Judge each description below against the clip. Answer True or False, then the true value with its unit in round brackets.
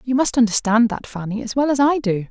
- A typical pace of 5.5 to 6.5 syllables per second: True (5.9 syllables/s)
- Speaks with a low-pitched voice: False (235 Hz)